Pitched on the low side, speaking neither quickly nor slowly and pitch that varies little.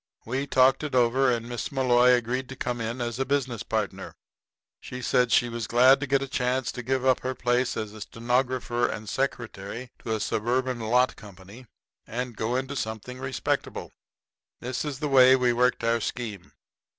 Yes: low, 125 Hz; average, 180 wpm; narrow, 1.9 semitones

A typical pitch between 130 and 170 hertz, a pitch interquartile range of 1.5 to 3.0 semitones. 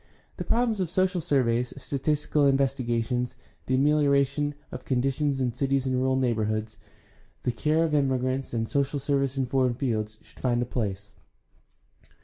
Yes: low, 135 Hz; average, 2.7 semitones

